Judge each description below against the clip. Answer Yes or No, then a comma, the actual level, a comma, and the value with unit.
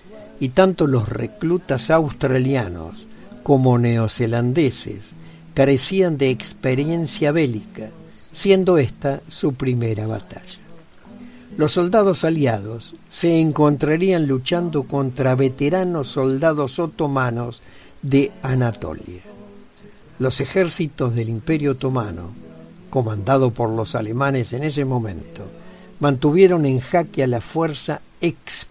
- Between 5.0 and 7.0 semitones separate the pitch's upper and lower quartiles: Yes, wide, 5.5 semitones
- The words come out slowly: Yes, slow, 100 wpm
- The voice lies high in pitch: No, medium, 140 Hz